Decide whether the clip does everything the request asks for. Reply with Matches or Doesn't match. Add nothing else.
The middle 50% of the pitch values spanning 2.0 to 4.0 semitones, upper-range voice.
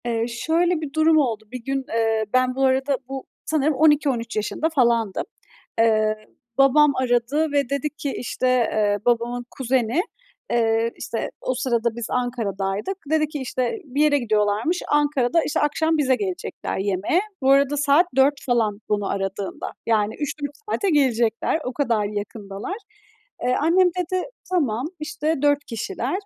Doesn't match